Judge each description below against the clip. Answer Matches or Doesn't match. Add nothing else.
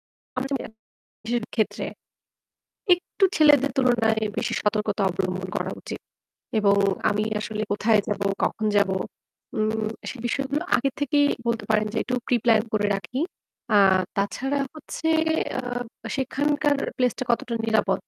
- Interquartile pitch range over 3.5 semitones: Matches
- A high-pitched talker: Matches